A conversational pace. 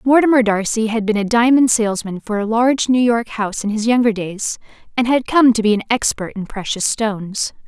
No: fast, 210 wpm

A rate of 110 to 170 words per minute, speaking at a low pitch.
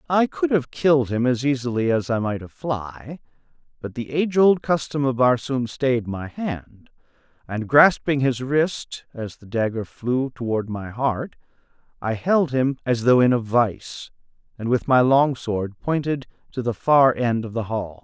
No: average, 180 wpm; low, 125 Hz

